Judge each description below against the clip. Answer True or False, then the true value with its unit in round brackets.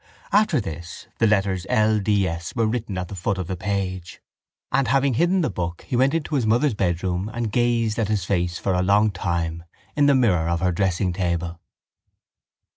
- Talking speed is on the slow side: False (195 wpm)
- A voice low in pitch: True (100 Hz)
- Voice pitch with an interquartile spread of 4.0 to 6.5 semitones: True (4.6 semitones)